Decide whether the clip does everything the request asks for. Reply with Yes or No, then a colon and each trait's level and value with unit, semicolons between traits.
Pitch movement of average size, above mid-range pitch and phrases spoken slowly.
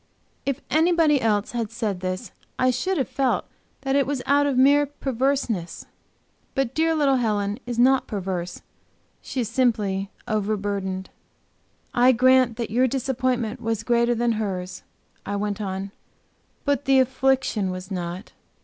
No: average, 4.7 semitones; high, 240 Hz; average, 145 wpm